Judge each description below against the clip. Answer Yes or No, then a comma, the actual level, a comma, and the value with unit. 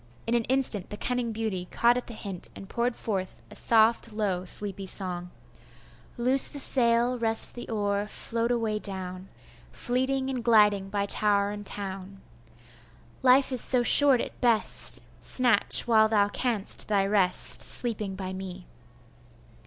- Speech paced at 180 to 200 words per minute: No, average, 150 wpm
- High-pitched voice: Yes, high, 215 Hz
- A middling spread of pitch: Yes, average, 3.5 semitones